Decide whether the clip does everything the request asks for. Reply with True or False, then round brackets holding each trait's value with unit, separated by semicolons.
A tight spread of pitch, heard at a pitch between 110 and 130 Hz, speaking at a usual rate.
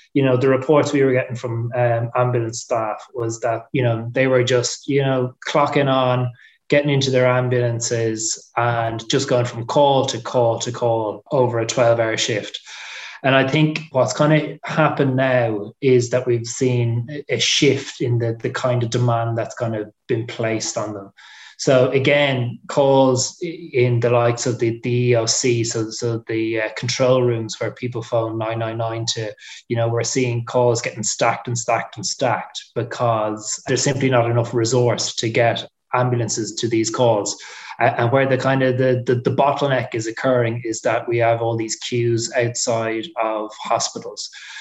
True (2.2 semitones; 120 Hz; 180 wpm)